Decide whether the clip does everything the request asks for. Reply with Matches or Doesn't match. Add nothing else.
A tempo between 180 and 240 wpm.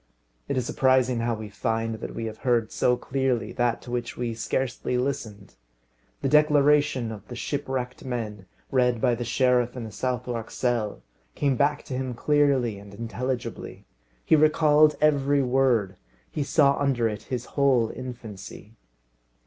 Doesn't match